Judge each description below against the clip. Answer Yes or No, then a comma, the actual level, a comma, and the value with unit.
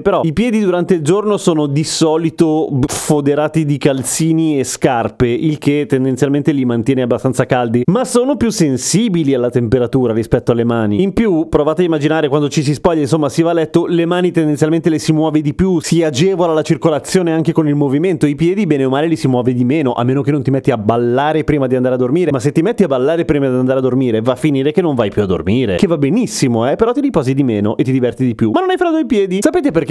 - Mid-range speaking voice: Yes, medium, 150 Hz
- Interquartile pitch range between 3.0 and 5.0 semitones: Yes, average, 4.4 semitones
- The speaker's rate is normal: No, fast, 250 wpm